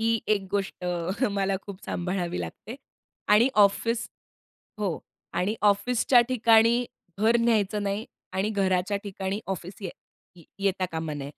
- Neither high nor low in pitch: No, high, 200 Hz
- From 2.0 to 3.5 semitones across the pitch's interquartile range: Yes, average, 2.9 semitones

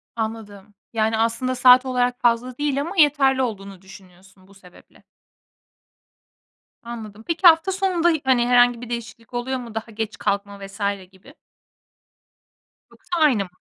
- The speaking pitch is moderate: No, high, 235 Hz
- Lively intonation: No, average, 4.3 semitones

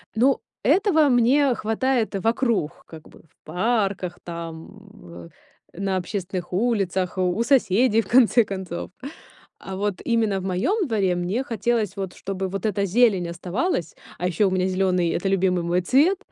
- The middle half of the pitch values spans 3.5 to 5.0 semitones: Yes, average, 4.5 semitones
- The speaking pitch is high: Yes, high, 195 Hz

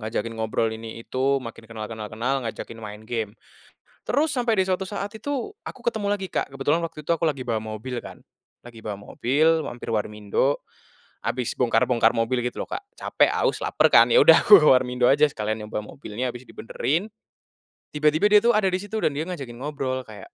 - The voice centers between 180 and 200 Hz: No, low, 130 Hz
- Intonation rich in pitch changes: Yes, wide, 6.4 semitones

